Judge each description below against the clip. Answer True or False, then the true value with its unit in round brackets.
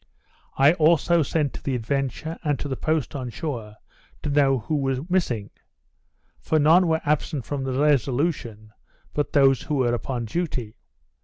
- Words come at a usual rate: True (160 wpm)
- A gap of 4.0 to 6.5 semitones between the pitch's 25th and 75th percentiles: False (3.6 semitones)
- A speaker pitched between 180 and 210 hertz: False (140 Hz)